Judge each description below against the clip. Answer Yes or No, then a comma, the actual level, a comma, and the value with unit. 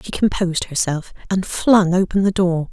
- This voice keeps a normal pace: Yes, average, 175 wpm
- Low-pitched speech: No, medium, 185 Hz